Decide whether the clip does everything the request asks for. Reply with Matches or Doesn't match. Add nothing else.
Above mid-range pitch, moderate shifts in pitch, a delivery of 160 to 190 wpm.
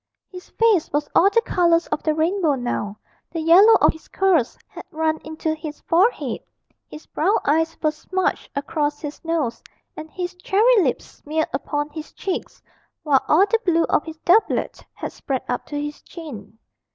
Matches